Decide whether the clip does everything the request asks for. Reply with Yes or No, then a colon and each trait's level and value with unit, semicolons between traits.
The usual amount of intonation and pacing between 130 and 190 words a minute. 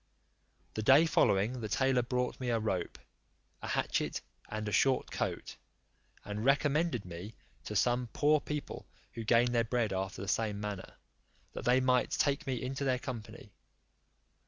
Yes: average, 3.8 semitones; average, 160 wpm